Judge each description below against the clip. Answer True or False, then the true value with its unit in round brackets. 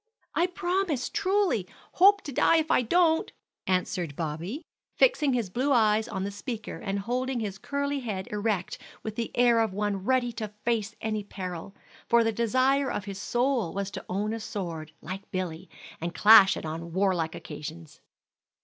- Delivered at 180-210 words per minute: False (170 wpm)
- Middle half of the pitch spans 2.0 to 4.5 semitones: False (5.3 semitones)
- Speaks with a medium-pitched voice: False (215 Hz)